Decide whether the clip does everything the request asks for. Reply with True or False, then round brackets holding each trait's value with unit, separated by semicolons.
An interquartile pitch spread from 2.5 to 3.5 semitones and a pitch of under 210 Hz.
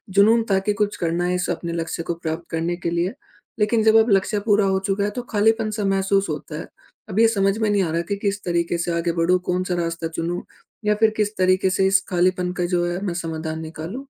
True (3.2 semitones; 185 Hz)